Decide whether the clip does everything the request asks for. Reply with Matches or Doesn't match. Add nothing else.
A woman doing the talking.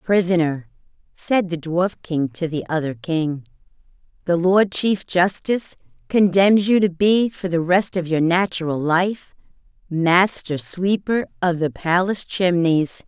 Matches